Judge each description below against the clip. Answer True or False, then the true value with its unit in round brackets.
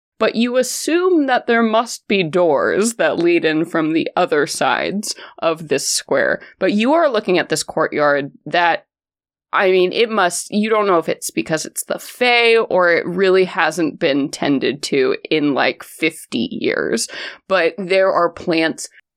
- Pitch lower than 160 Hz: False (190 Hz)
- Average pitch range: False (6.2 semitones)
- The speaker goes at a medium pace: True (170 wpm)